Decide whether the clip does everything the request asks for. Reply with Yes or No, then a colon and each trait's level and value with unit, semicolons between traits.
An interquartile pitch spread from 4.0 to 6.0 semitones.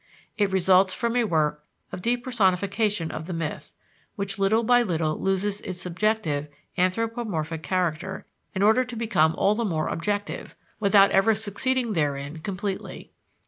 Yes: average, 4.7 semitones